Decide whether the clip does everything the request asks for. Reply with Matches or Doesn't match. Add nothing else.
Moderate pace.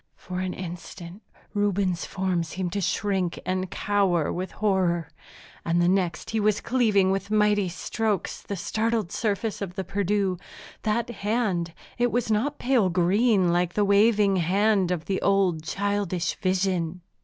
Matches